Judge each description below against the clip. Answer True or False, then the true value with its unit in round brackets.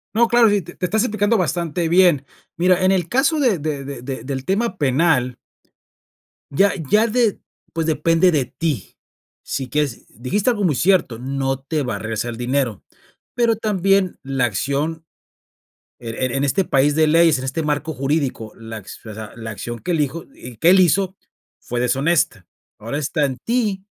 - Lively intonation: True (6.3 semitones)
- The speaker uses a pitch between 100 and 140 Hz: False (155 Hz)